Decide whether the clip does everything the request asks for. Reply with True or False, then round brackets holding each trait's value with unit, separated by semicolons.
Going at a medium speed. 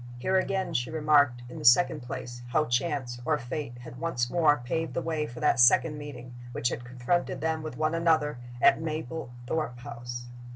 True (180 wpm)